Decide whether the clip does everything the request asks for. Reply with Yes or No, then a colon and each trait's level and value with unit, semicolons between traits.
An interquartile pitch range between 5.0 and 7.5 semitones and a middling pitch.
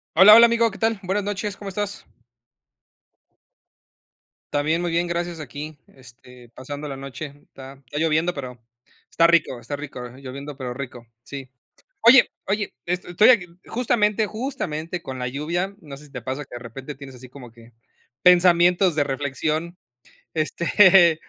Yes: wide, 5.5 semitones; medium, 155 Hz